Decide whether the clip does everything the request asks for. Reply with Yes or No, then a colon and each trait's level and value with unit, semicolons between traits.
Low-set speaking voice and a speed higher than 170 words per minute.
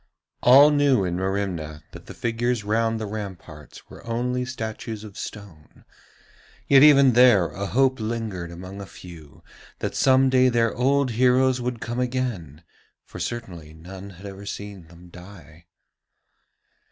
No: low, 110 Hz; average, 145 wpm